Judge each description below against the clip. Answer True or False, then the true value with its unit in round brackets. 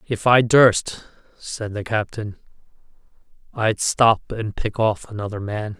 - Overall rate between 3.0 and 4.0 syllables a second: True (3.8 syllables/s)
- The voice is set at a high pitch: False (110 Hz)